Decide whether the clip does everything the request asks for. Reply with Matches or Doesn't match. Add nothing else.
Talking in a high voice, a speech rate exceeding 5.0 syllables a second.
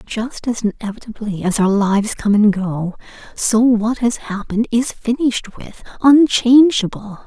Doesn't match